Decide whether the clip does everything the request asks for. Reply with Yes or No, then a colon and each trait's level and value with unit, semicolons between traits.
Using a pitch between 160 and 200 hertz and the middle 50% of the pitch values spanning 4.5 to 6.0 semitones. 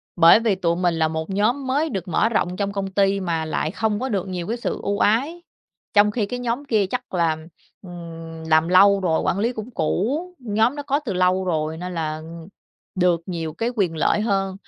Yes: high, 195 Hz; average, 4.8 semitones